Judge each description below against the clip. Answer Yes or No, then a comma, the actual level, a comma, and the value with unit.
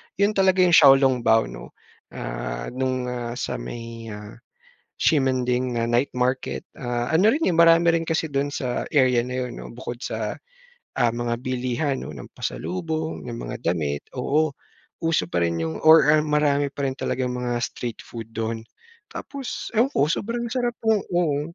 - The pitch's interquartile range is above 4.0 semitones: Yes, average, 5.2 semitones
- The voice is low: Yes, low, 130 Hz